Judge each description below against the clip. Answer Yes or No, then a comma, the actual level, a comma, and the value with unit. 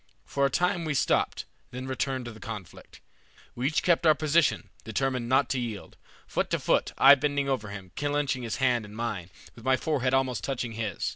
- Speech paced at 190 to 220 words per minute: Yes, average, 200 wpm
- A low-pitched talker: Yes, low, 130 Hz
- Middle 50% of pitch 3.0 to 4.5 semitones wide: Yes, average, 3.5 semitones